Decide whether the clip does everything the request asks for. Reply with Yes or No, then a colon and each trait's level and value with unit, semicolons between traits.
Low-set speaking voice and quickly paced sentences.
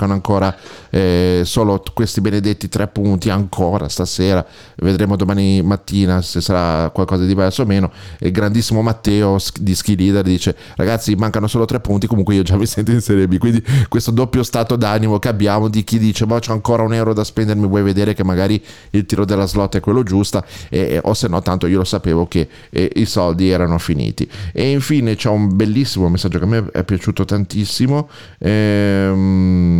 Yes: low, 100 Hz; fast, 190 wpm